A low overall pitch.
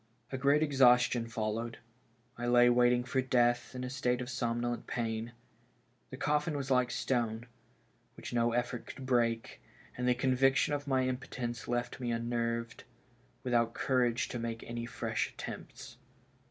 Yes: low, 120 Hz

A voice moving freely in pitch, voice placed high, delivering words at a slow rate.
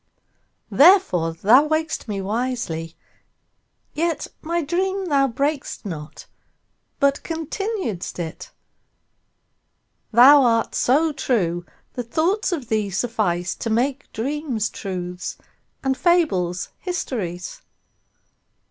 Yes: wide, 8.6 semitones; very high, 250 Hz; slow, 85 wpm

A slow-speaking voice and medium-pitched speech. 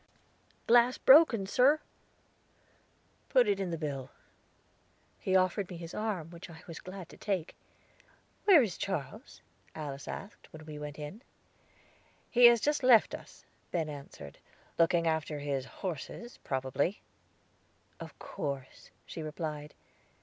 Yes: slow, 130 wpm; medium, 170 Hz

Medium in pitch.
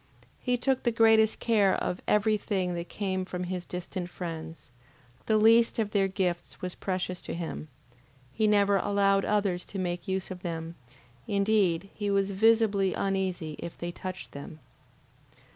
No: high, 195 Hz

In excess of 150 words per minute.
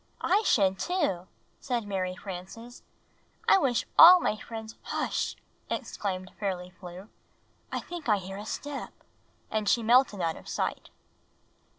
No: average, 145 wpm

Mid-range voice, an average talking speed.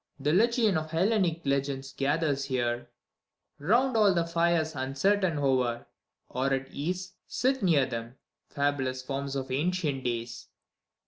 No: medium, 145 Hz; slow, 130 wpm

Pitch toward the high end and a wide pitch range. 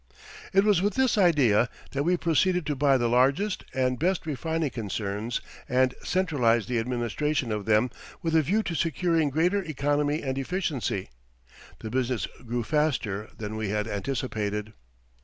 No: low, 135 Hz; wide, 6.1 semitones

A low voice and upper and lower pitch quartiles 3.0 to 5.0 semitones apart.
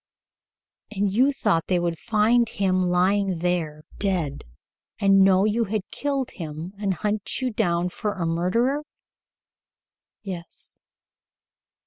No: high, 195 Hz; average, 3.6 semitones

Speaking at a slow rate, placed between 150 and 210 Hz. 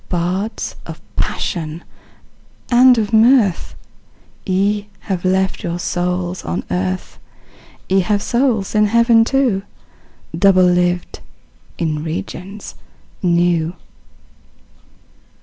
Yes: slow, 95 wpm; medium, 185 Hz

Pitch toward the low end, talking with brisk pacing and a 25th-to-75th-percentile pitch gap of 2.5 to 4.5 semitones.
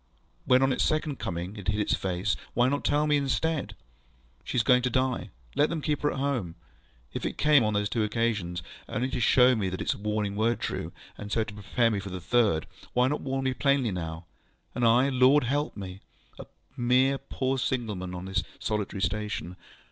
No: low, 115 Hz; fast, 210 wpm; average, 4.9 semitones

